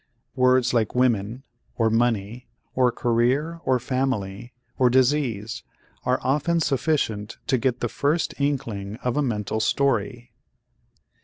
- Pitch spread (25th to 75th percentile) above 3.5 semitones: No, average, 2.9 semitones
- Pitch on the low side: Yes, low, 125 Hz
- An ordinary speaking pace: No, slow, 125 wpm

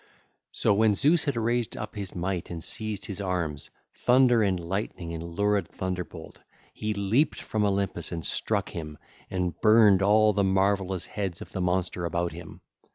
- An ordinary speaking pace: Yes, average, 165 wpm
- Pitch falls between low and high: No, very low, 95 Hz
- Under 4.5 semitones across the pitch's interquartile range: Yes, average, 3.3 semitones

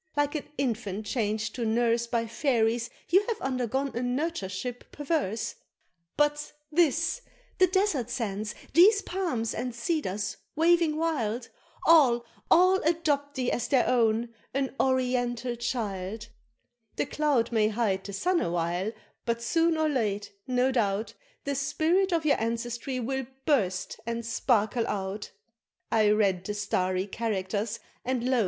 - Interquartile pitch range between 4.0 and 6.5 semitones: Yes, average, 5.2 semitones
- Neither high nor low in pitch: No, high, 240 Hz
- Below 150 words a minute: Yes, slow, 135 wpm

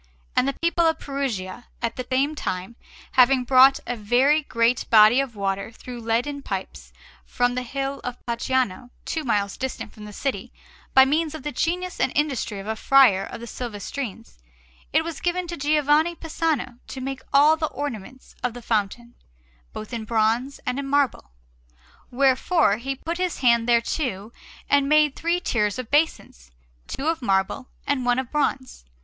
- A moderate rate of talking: Yes, average, 170 wpm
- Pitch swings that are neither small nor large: Yes, average, 4.0 semitones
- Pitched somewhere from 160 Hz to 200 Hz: No, very high, 255 Hz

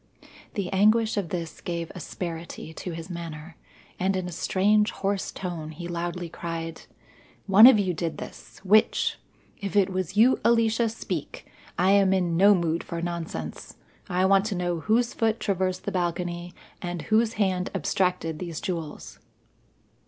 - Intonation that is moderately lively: Yes, average, 3.0 semitones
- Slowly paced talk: No, average, 155 wpm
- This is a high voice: No, medium, 180 Hz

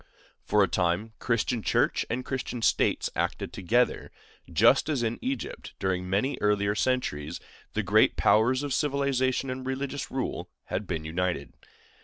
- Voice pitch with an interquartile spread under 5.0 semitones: No, wide, 5.4 semitones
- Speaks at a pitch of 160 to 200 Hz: No, low, 115 Hz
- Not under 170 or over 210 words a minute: No, average, 145 wpm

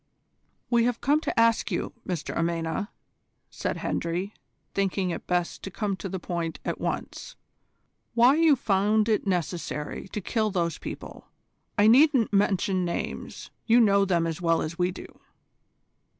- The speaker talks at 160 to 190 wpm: No, average, 150 wpm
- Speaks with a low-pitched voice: No, high, 195 Hz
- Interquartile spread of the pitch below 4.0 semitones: No, average, 4.5 semitones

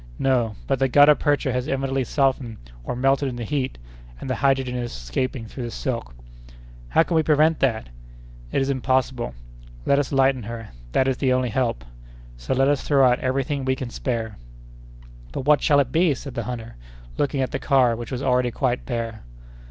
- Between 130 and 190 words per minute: No, average, 200 wpm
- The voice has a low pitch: Yes, low, 130 Hz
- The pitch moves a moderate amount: No, narrow, 2.3 semitones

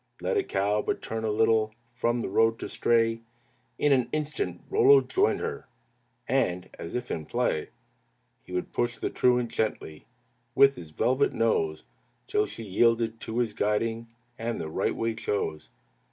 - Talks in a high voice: No, low, 115 Hz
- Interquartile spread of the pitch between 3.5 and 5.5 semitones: No, average, 2.7 semitones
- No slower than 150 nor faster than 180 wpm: Yes, average, 165 wpm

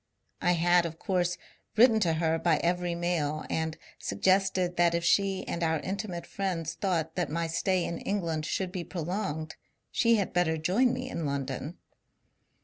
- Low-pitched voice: No, medium, 175 Hz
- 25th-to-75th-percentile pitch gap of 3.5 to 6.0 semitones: No, average, 2.7 semitones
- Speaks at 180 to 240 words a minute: No, average, 165 wpm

